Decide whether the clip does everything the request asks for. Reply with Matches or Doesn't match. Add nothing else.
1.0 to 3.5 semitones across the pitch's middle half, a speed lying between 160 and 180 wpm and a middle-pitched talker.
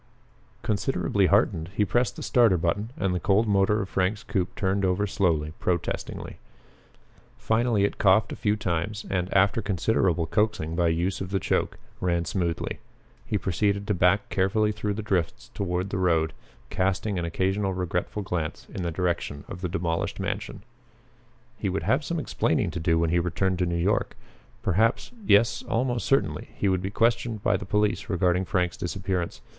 Doesn't match